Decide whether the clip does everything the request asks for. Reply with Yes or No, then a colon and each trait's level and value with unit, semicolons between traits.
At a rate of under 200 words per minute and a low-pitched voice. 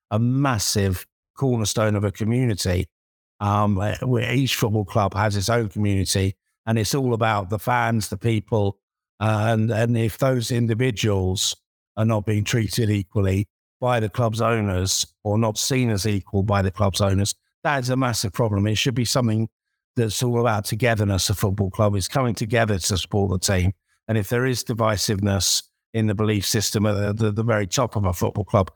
Yes: average, 185 wpm; low, 110 Hz